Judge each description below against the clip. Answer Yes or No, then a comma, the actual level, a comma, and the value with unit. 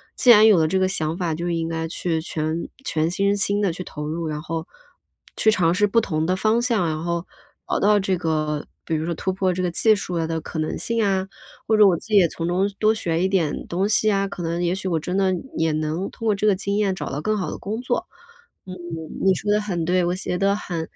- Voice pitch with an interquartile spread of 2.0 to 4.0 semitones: Yes, average, 3.5 semitones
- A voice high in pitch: No, medium, 180 Hz